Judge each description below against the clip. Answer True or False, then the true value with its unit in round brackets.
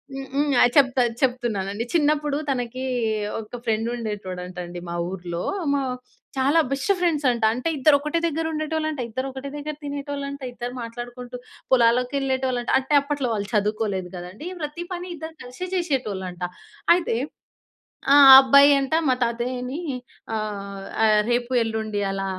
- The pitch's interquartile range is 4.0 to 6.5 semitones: True (4.7 semitones)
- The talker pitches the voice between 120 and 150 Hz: False (250 Hz)